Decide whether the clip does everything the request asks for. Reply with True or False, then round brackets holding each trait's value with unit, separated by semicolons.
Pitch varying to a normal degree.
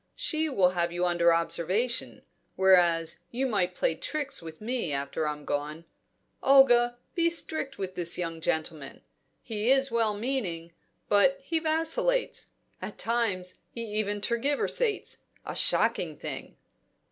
False (7.8 semitones)